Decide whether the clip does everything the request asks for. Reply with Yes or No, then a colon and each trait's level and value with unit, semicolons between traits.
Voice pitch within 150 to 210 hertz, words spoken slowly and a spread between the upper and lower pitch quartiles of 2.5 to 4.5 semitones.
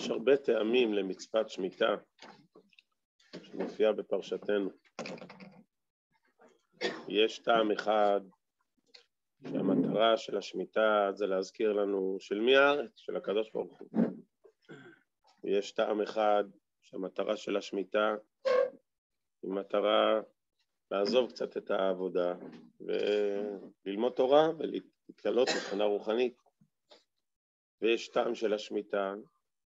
No: low, 105 Hz; slow, 90 wpm; average, 3.7 semitones